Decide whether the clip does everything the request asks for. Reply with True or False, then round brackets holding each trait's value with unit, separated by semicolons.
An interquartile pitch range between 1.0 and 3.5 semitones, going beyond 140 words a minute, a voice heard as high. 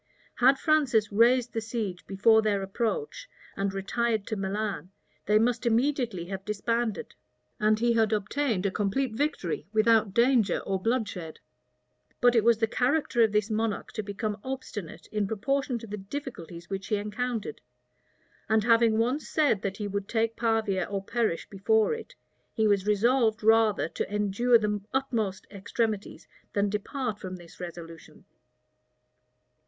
True (3.0 semitones; 150 wpm; 220 Hz)